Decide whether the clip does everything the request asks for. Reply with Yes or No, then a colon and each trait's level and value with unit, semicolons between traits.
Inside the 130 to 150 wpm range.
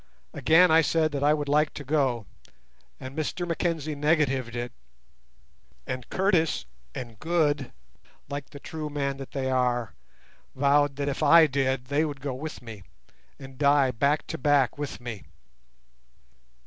Yes: average, 145 wpm